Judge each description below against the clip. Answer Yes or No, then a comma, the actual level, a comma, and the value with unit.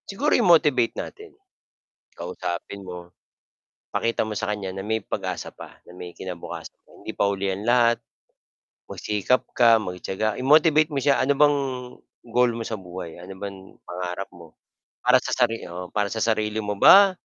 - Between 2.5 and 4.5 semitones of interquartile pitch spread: No, average, 4.9 semitones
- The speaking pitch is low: Yes, low, 105 Hz